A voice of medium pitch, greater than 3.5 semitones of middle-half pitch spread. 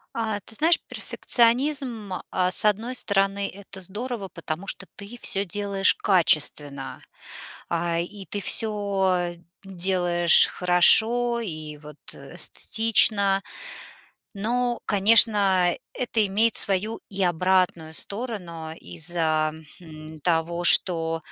No: high, 195 Hz; average, 4.0 semitones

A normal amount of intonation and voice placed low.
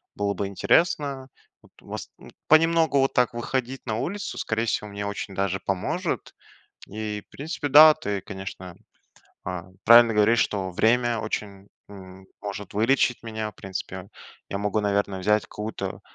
Yes: average, 3.8 semitones; low, 105 Hz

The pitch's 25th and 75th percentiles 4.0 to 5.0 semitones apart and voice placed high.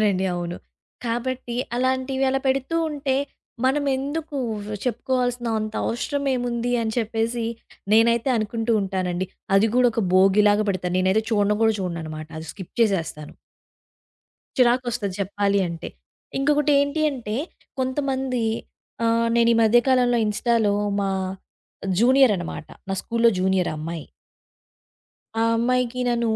Yes: average, 4.3 semitones; high, 230 Hz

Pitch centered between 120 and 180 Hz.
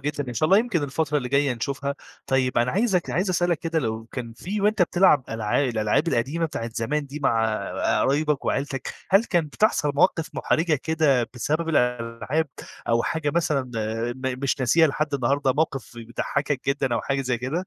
Yes: medium, 140 Hz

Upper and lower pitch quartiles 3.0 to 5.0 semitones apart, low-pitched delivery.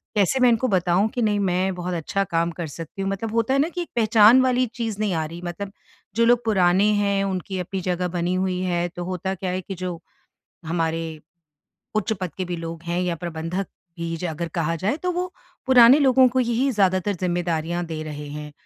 No: average, 4.2 semitones; medium, 185 Hz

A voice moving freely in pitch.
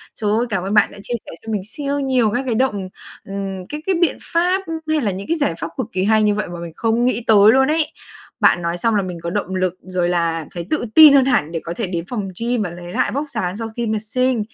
Yes: wide, 5.7 semitones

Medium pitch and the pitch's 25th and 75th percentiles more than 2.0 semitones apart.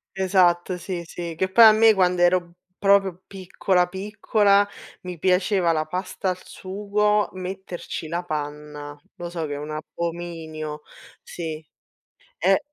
Yes: medium, 180 Hz; average, 2.7 semitones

